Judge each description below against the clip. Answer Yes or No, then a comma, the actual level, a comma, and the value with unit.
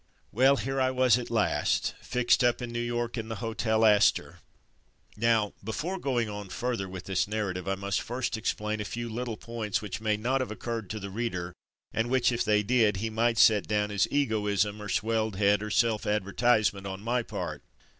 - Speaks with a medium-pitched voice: No, low, 110 Hz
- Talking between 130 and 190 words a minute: No, average, 200 wpm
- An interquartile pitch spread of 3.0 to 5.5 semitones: No, narrow, 2.5 semitones